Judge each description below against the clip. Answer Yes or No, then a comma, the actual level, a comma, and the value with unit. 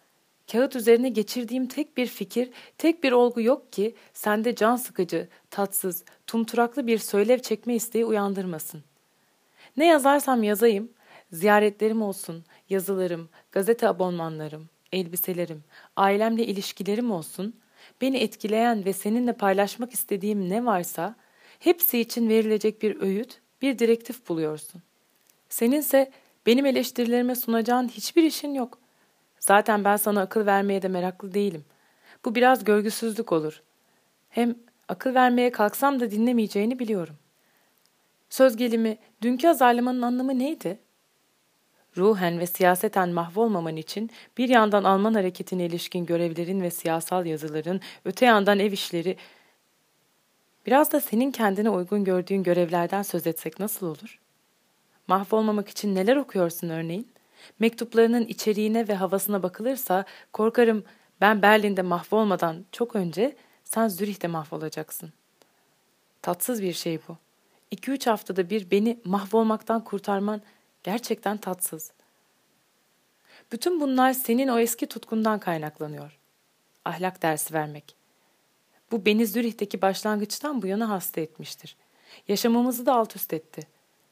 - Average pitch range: Yes, average, 4.2 semitones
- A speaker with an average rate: Yes, average, 120 wpm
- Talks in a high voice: Yes, high, 210 Hz